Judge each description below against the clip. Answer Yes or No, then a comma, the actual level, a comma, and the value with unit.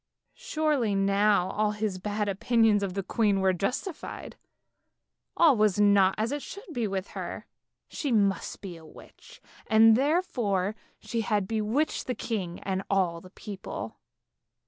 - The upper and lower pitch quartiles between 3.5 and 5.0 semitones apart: No, average, 3.0 semitones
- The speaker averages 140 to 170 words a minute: Yes, average, 145 wpm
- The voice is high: Yes, high, 210 Hz